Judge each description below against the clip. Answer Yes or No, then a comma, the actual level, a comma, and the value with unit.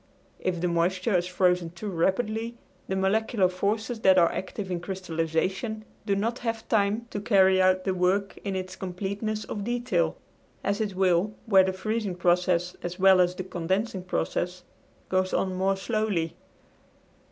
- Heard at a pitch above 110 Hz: Yes, high, 190 Hz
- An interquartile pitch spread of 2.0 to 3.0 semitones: Yes, narrow, 2.5 semitones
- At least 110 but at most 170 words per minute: Yes, average, 160 wpm